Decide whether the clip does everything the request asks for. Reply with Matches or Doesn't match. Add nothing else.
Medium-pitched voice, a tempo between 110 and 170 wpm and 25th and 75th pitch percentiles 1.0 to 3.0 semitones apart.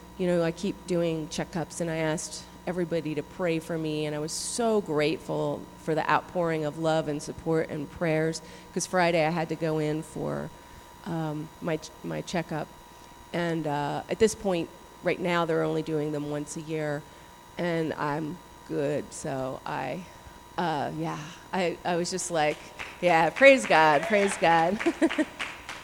Matches